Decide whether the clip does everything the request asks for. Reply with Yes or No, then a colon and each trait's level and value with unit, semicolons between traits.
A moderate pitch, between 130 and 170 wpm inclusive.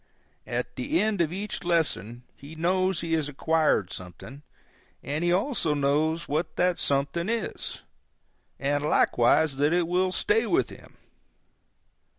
Yes: medium, 160 Hz; average, 140 wpm